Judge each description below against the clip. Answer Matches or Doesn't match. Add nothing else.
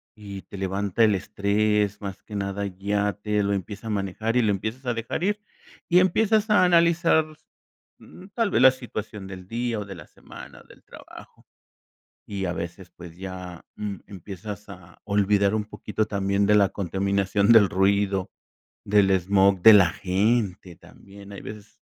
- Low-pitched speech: Matches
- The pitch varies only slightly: Matches